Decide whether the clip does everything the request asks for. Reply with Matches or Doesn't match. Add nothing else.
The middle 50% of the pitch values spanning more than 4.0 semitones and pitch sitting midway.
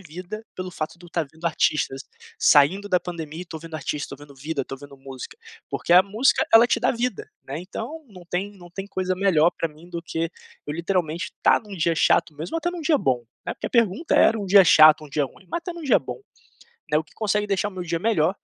Matches